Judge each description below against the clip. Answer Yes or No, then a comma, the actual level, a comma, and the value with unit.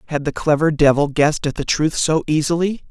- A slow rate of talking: No, fast, 205 wpm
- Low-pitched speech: No, medium, 150 Hz